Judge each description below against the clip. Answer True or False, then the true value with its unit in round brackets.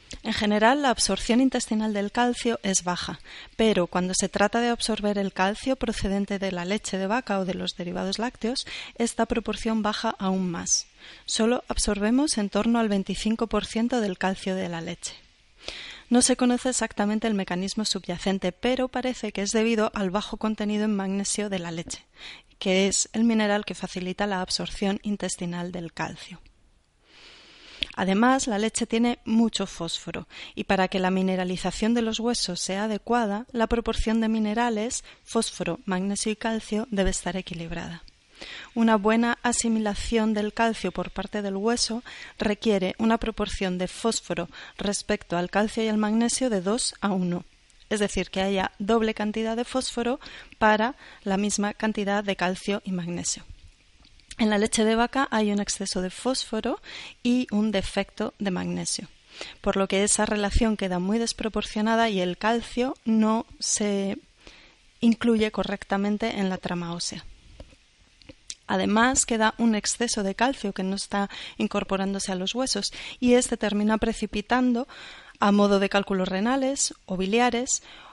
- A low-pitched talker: False (210 Hz)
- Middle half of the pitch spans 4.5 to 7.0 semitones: False (3.0 semitones)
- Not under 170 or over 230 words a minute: False (155 wpm)